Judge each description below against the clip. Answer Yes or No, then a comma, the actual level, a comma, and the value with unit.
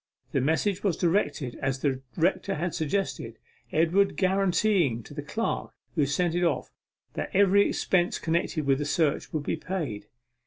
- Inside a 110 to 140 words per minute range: No, average, 160 wpm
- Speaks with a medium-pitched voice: Yes, medium, 165 Hz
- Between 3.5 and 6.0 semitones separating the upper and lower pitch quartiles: Yes, average, 4.9 semitones